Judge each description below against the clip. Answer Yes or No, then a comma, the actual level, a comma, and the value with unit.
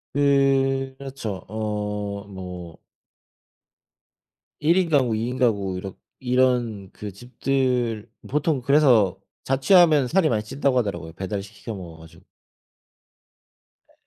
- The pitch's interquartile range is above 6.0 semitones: No, average, 5.2 semitones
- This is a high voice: No, low, 115 Hz